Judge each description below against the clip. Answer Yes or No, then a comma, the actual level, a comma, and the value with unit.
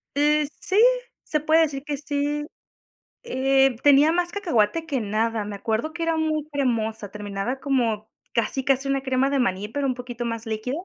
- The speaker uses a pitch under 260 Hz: No, very high, 270 Hz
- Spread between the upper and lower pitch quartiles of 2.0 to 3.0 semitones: No, average, 4.7 semitones